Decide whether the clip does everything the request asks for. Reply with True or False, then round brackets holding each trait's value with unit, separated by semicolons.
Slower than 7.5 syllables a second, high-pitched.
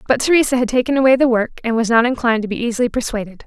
False (7.8 syllables/s; 240 Hz)